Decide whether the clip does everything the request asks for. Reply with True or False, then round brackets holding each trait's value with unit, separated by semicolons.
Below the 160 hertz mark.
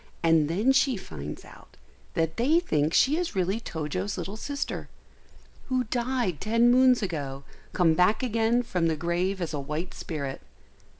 False (190 Hz)